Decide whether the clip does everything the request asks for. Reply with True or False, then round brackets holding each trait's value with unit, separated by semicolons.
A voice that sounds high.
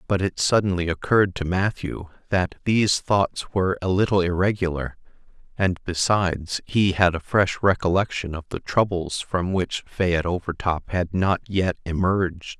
False (90 Hz)